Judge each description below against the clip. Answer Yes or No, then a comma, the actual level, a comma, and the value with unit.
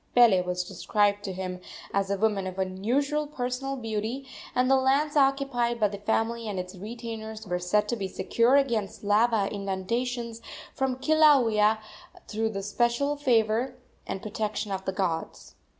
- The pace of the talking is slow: No, average, 155 wpm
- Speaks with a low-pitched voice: No, high, 220 Hz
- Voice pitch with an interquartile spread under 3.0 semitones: No, average, 4.1 semitones